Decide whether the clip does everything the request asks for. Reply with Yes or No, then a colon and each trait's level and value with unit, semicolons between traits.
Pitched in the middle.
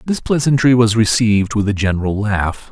No: low, 110 Hz